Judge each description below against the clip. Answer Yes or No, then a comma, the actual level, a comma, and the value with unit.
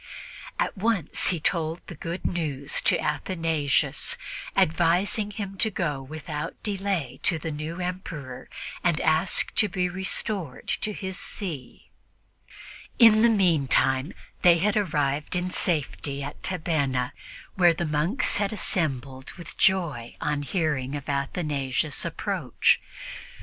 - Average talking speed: No, slow, 125 wpm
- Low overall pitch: No, medium, 165 Hz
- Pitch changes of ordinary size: Yes, average, 4.5 semitones